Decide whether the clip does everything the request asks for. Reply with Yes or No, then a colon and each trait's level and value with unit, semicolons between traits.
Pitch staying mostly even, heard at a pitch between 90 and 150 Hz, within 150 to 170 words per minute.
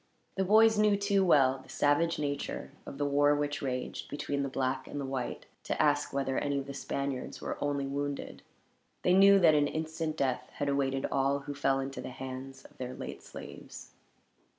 No: narrow, 2.1 semitones; medium, 140 Hz; average, 195 wpm